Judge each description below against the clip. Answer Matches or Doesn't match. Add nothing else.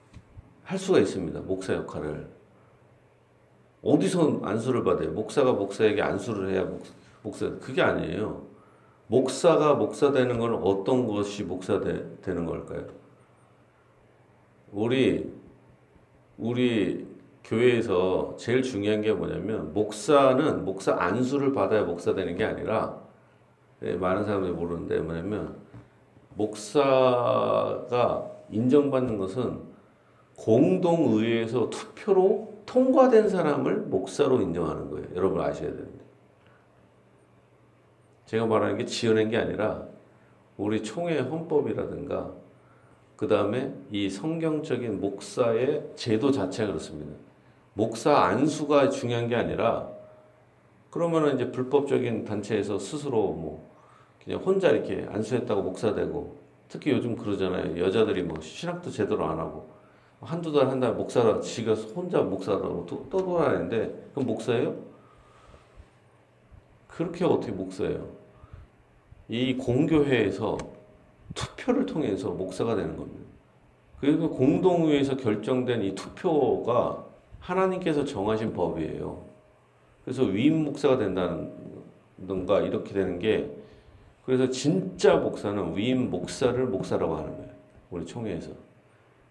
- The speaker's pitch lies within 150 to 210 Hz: Doesn't match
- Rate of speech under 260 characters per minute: Doesn't match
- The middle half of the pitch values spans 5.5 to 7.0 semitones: Matches